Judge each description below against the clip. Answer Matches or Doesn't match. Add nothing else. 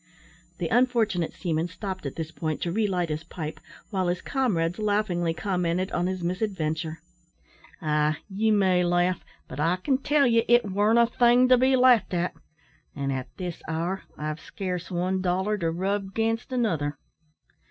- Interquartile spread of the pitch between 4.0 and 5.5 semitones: Matches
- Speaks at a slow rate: Doesn't match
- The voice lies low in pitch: Doesn't match